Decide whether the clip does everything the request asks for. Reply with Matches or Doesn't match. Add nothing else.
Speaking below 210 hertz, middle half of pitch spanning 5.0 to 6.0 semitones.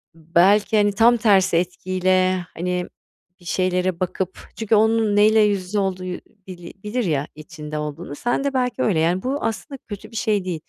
Doesn't match